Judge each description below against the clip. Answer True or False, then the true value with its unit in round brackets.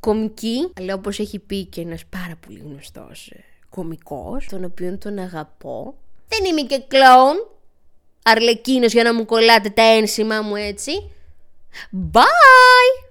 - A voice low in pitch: False (215 Hz)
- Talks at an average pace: True (135 wpm)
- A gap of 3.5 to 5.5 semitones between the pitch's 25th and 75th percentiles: True (5.1 semitones)